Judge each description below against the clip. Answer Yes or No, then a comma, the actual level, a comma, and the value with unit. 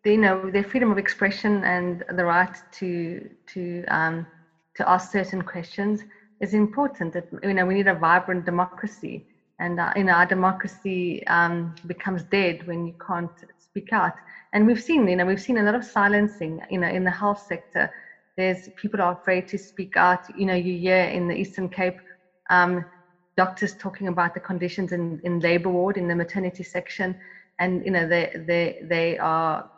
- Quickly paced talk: No, average, 190 wpm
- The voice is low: No, medium, 180 Hz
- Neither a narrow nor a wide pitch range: No, narrow, 2.0 semitones